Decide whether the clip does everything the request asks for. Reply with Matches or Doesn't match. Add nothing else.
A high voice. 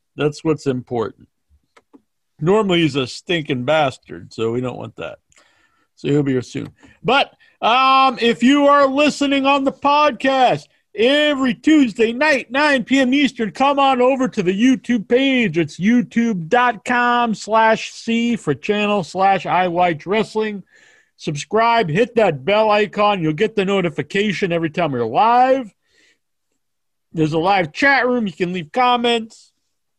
Matches